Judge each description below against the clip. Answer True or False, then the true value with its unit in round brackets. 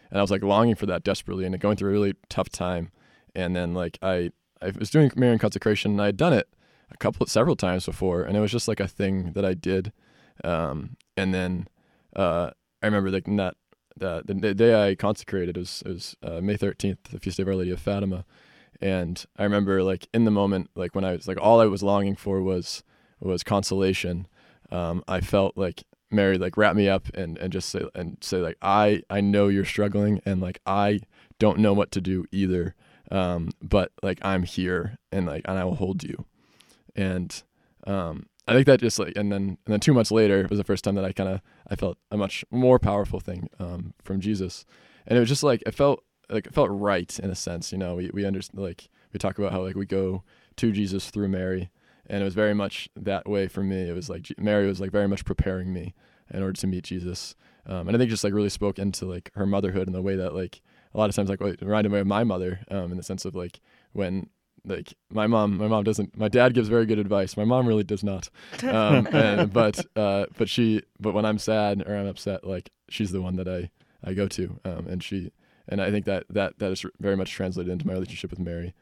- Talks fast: True (240 wpm)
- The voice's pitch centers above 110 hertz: False (95 Hz)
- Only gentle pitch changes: True (1.8 semitones)